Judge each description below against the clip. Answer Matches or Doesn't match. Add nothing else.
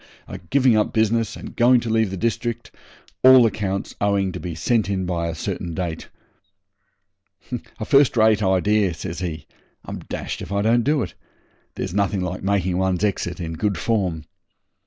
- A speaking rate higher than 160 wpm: Matches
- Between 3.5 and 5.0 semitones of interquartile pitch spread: Matches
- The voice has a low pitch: Matches